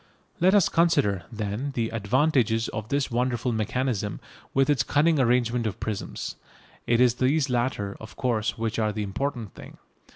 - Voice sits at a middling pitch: No, low, 120 Hz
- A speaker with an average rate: Yes, average, 160 wpm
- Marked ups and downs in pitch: No, average, 3.7 semitones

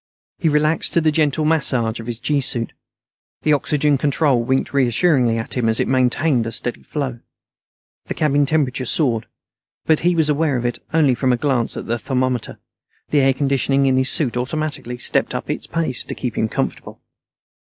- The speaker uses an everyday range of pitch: Yes, average, 3.7 semitones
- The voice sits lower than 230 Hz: Yes, low, 135 Hz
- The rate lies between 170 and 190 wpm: Yes, average, 185 wpm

